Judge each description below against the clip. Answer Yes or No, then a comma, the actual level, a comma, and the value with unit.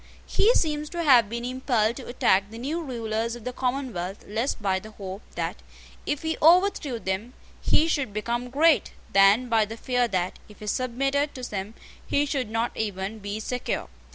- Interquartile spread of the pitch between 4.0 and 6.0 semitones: Yes, average, 4.4 semitones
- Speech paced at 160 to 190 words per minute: Yes, average, 180 wpm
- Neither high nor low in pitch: No, high, 235 Hz